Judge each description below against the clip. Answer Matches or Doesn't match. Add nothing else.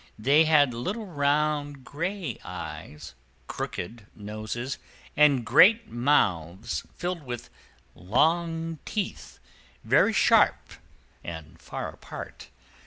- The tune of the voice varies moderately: Doesn't match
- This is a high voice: Doesn't match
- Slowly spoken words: Matches